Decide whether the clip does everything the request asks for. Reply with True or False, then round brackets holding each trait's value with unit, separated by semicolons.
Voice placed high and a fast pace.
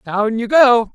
False (235 Hz; 190 wpm)